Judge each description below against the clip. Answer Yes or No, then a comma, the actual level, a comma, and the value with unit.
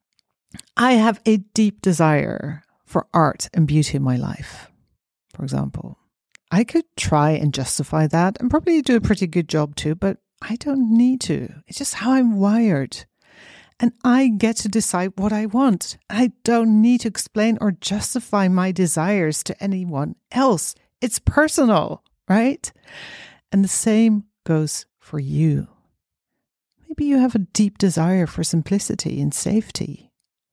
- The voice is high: Yes, high, 205 Hz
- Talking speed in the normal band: Yes, average, 150 wpm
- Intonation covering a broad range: Yes, wide, 6.2 semitones